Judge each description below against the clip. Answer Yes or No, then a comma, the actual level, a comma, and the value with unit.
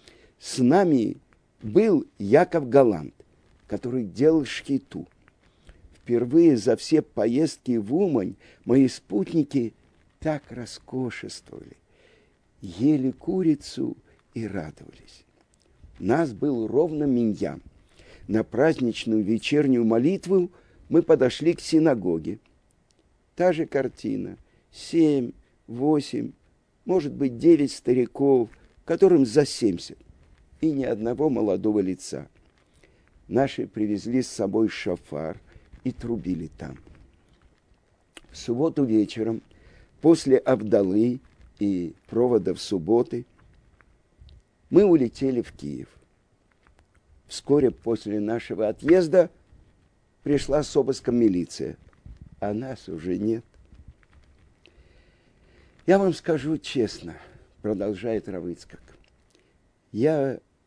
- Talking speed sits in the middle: No, slow, 90 wpm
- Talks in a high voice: No, low, 115 Hz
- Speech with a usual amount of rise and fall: No, wide, 7.0 semitones